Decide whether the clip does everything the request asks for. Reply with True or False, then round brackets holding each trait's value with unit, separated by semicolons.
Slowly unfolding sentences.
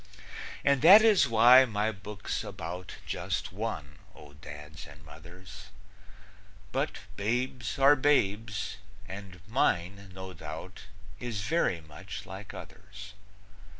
True (115 wpm)